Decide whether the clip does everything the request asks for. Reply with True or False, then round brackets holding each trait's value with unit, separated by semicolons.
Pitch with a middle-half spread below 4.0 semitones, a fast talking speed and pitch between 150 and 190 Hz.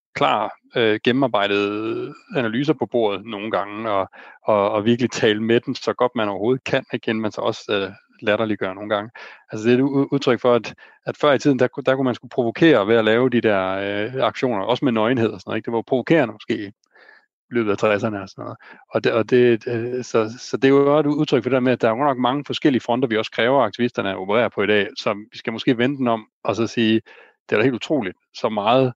False (3.0 semitones; 245 wpm; 120 Hz)